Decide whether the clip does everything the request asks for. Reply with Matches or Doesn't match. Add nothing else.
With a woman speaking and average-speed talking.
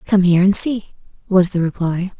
Matches